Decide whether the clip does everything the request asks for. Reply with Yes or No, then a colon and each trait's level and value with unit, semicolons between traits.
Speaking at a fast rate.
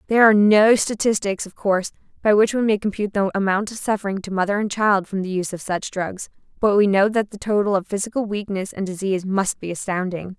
Yes: fast, 225 wpm